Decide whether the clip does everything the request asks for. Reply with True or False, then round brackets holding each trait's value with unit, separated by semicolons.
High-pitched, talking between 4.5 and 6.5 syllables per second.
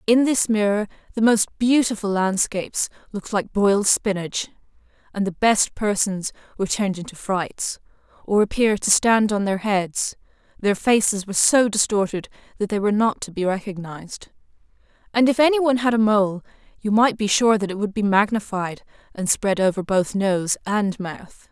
True (205 Hz; 5.1 syllables/s)